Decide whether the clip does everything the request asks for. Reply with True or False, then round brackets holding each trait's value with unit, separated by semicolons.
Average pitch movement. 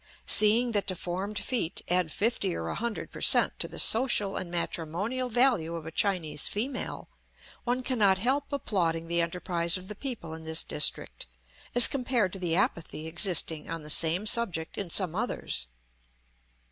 False (5.8 semitones)